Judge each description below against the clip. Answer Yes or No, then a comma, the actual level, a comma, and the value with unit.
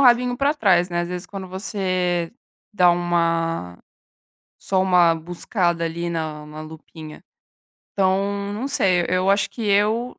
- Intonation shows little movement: No, average, 3.1 semitones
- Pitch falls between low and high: Yes, medium, 180 Hz